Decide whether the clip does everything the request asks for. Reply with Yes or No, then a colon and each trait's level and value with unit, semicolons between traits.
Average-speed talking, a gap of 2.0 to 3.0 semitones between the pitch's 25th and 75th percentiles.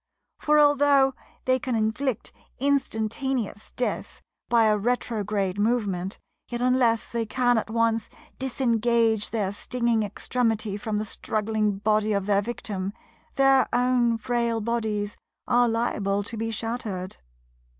No: slow, 125 wpm; average, 2.7 semitones